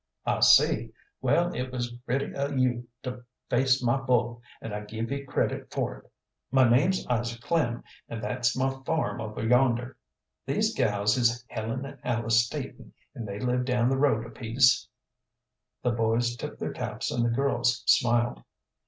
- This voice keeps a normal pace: Yes, average, 170 wpm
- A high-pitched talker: No, low, 120 Hz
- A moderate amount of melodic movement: No, narrow, 1.9 semitones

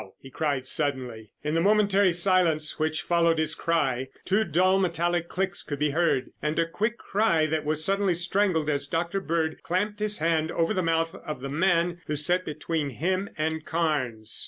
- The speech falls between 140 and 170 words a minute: No, average, 180 wpm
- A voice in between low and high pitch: Yes, medium, 165 Hz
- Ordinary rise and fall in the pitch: Yes, average, 3.3 semitones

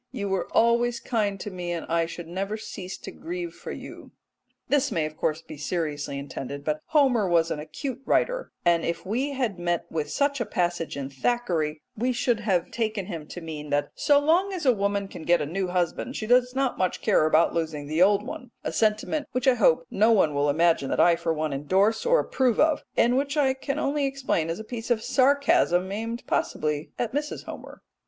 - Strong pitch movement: Yes, wide, 7.4 semitones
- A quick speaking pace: Yes, fast, 215 wpm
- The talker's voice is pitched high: Yes, high, 200 Hz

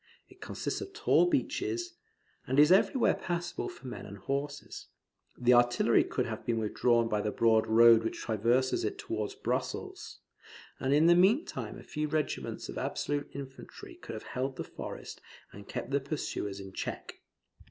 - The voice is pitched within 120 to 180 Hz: Yes, medium, 140 Hz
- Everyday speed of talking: Yes, average, 165 wpm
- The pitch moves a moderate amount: No, wide, 8.7 semitones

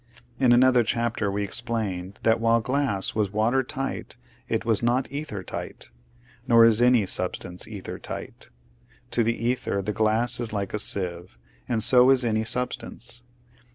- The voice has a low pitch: Yes, low, 115 Hz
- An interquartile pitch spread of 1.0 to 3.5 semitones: Yes, average, 2.9 semitones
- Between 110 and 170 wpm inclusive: Yes, average, 155 wpm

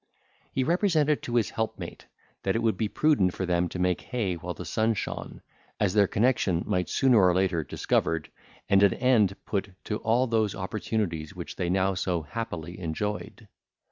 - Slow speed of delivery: No, average, 180 wpm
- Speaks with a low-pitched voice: Yes, low, 100 Hz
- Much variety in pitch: No, average, 4.1 semitones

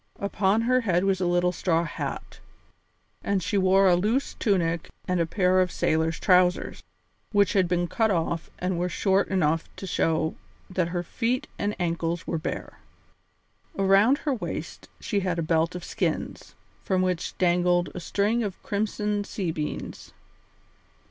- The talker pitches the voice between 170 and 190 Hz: Yes, medium, 185 Hz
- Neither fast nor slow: Yes, average, 160 wpm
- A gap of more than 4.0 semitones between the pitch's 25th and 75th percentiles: No, average, 2.7 semitones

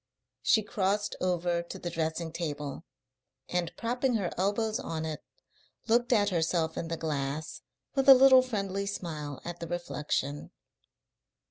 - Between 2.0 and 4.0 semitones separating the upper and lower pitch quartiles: No, average, 4.7 semitones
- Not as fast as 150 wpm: Yes, average, 140 wpm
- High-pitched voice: No, medium, 175 Hz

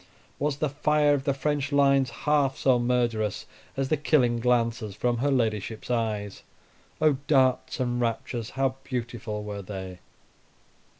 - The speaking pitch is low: Yes, low, 125 Hz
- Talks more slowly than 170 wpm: Yes, average, 140 wpm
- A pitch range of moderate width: Yes, average, 3.5 semitones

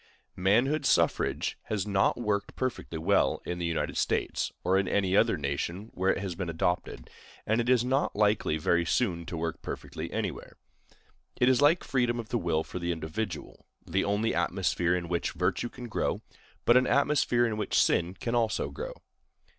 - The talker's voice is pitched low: Yes, low, 100 Hz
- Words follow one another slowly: No, average, 180 wpm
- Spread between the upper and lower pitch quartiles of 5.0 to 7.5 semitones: Yes, wide, 5.6 semitones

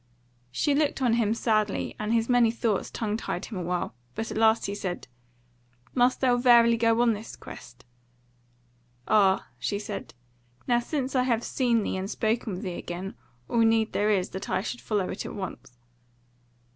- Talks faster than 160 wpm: Yes, average, 185 wpm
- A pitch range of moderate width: Yes, average, 3.1 semitones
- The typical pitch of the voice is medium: No, high, 225 Hz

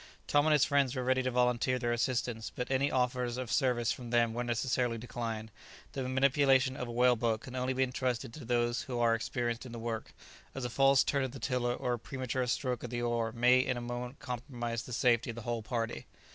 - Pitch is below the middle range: Yes, low, 125 Hz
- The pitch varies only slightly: Yes, narrow, 1.6 semitones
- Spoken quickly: Yes, fast, 230 wpm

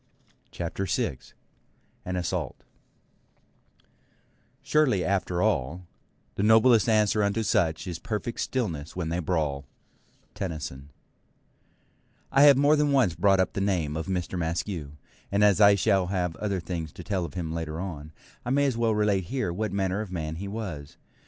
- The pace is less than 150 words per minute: No, average, 160 wpm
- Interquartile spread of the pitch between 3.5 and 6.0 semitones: Yes, average, 4.4 semitones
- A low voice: Yes, very low, 95 Hz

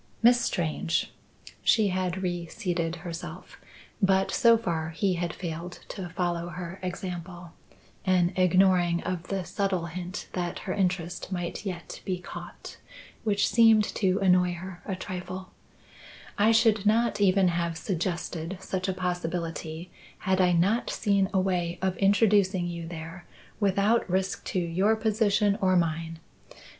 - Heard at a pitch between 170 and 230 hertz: Yes, medium, 185 Hz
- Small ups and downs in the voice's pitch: Yes, narrow, 2.2 semitones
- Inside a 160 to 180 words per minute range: No, average, 140 wpm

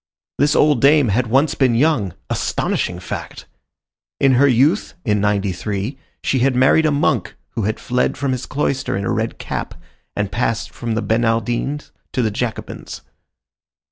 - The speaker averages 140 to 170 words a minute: Yes, average, 155 wpm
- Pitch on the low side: Yes, low, 120 Hz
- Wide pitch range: No, average, 4.2 semitones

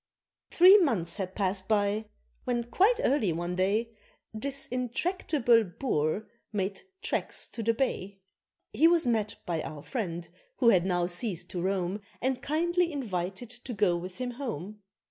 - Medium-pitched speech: No, high, 215 Hz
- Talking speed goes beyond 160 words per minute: No, average, 150 wpm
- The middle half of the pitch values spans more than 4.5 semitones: Yes, wide, 5.6 semitones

